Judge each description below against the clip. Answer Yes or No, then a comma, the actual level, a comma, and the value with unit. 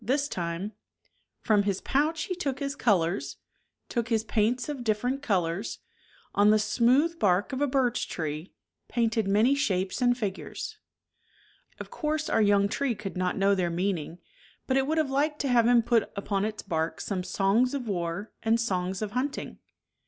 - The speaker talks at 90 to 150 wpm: No, average, 175 wpm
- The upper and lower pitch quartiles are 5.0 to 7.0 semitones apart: Yes, average, 5.3 semitones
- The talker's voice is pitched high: Yes, high, 220 Hz